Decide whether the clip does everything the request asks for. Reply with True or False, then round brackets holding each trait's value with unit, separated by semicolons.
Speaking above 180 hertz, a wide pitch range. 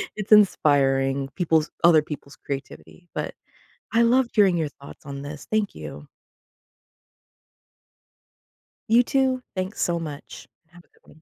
False (165 Hz; 7.0 semitones)